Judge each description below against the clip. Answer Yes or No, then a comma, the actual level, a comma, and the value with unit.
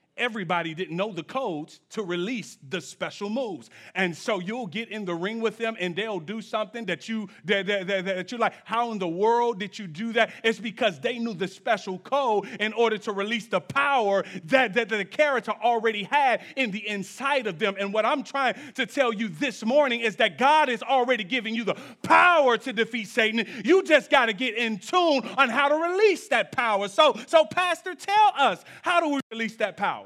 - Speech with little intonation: No, average, 4.5 semitones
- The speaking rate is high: Yes, fast, 215 wpm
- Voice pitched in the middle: No, high, 225 Hz